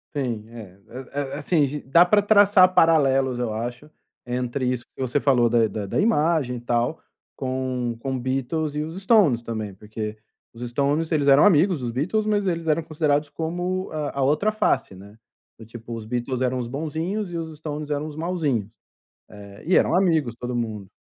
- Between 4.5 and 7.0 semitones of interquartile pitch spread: Yes, average, 5.1 semitones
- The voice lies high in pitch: No, medium, 140 Hz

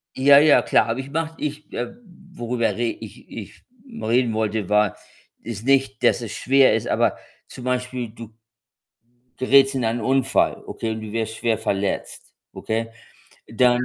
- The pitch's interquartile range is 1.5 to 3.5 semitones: Yes, average, 3.2 semitones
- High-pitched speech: No, low, 120 Hz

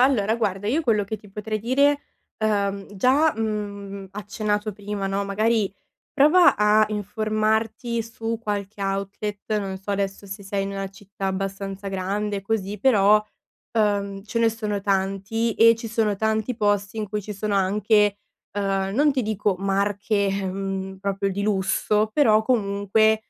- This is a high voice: Yes, high, 205 Hz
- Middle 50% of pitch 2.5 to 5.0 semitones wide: No, narrow, 1.9 semitones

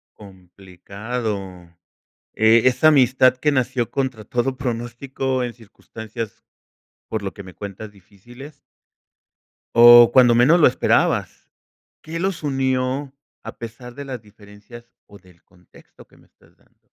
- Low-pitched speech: Yes, low, 120 Hz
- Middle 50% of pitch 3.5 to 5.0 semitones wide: Yes, average, 3.9 semitones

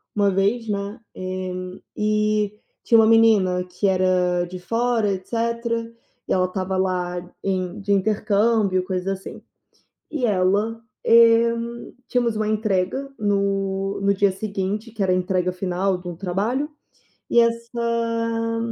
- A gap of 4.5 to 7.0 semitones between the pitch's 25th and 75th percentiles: No, average, 3.5 semitones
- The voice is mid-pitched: No, high, 200 Hz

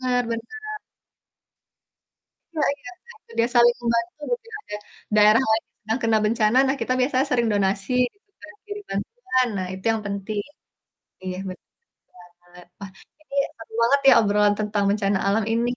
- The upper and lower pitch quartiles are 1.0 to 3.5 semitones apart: No, average, 3.9 semitones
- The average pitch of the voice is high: Yes, high, 230 Hz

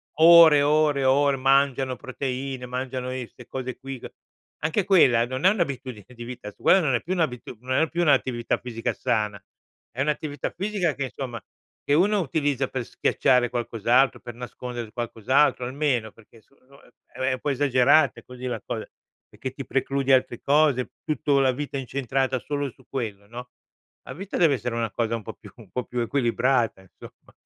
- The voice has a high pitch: No, low, 130 Hz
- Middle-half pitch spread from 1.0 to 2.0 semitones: No, average, 2.8 semitones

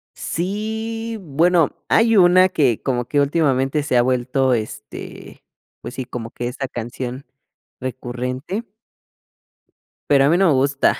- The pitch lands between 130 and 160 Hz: Yes, medium, 140 Hz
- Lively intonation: Yes, wide, 5.9 semitones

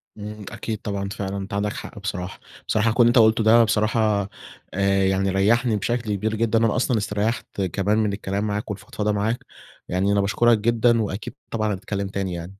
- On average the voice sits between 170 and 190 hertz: No, low, 105 Hz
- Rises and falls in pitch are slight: Yes, narrow, 2.2 semitones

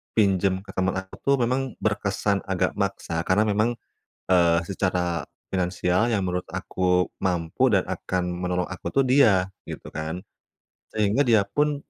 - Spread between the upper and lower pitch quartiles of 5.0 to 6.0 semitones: No, average, 3.0 semitones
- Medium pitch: No, very low, 95 Hz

